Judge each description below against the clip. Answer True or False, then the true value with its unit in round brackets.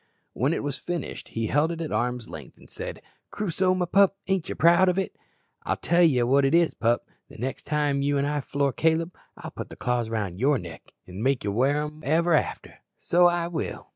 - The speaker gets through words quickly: True (230 wpm)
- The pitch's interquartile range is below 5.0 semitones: False (5.3 semitones)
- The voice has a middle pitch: True (145 Hz)